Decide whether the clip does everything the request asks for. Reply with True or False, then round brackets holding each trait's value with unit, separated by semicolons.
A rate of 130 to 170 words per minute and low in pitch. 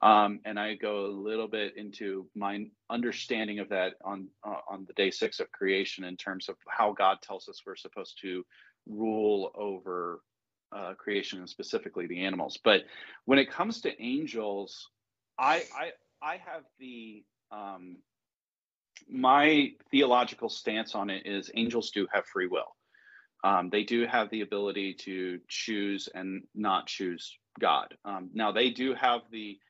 True (160 wpm; 105 Hz)